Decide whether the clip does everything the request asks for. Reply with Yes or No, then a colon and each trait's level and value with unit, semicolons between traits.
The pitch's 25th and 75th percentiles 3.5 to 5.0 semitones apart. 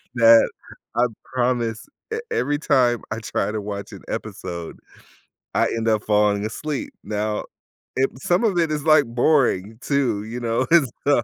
Yes: average, 4.7 semitones